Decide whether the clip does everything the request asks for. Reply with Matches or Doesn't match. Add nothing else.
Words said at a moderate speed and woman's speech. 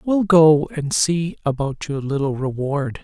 Doesn't match